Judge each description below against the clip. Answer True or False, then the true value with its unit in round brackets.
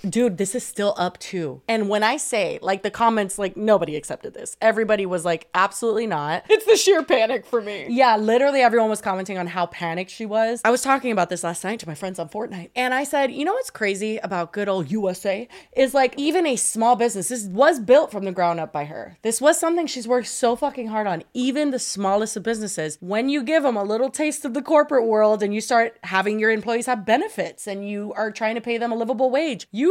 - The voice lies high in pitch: True (225 Hz)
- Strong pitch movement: False (4.7 semitones)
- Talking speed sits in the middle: False (240 wpm)